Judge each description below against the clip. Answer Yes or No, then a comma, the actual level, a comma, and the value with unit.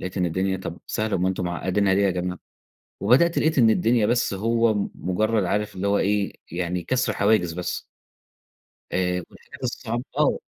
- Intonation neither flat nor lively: Yes, average, 3.5 semitones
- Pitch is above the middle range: No, low, 100 Hz